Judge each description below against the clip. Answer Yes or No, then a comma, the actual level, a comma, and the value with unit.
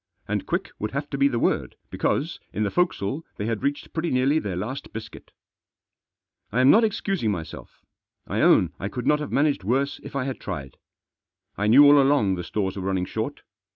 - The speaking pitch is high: No, low, 125 Hz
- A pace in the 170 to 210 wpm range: Yes, average, 200 wpm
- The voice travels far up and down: Yes, wide, 6.1 semitones